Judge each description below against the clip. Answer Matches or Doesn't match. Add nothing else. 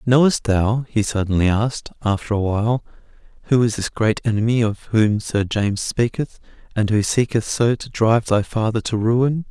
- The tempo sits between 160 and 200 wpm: Matches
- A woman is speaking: Doesn't match